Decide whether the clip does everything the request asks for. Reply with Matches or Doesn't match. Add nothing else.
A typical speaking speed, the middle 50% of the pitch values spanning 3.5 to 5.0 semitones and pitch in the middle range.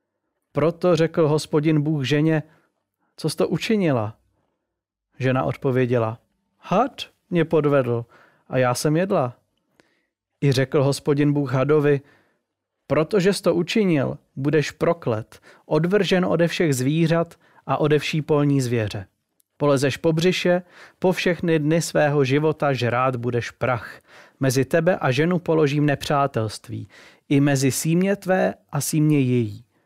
Matches